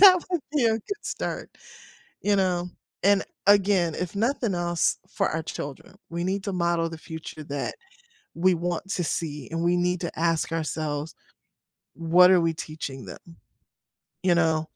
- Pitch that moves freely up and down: No, average, 2.7 semitones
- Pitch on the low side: No, medium, 175 Hz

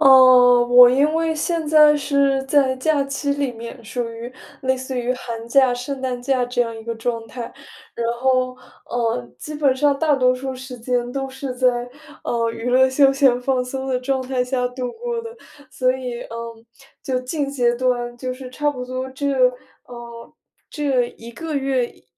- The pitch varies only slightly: Yes, narrow, 2.0 semitones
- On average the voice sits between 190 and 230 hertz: No, very high, 255 Hz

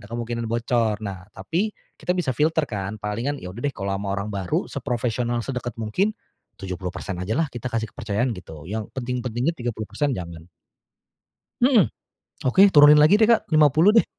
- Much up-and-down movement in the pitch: Yes, wide, 6.3 semitones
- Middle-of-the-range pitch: No, low, 120 Hz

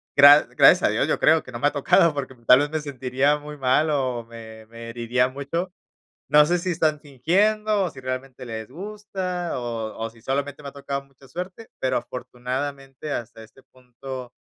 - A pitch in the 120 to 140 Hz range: Yes, low, 135 Hz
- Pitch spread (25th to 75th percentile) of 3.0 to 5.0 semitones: Yes, average, 3.5 semitones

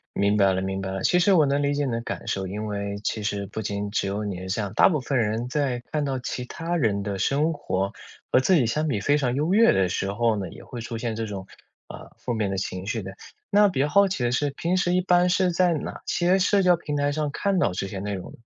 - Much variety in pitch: Yes, wide, 7.3 semitones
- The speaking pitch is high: No, low, 120 Hz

